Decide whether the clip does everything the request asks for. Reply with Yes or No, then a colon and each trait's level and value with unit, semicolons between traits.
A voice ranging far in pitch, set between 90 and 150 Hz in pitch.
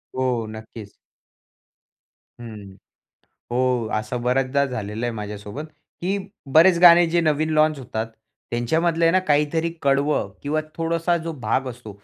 Yes: wide, 5.7 semitones; low, 135 Hz